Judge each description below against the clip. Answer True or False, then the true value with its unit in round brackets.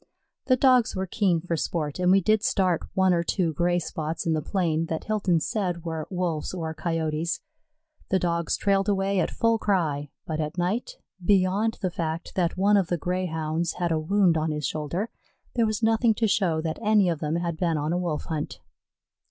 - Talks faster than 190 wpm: True (200 wpm)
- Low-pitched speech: False (175 Hz)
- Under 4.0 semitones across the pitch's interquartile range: True (3.4 semitones)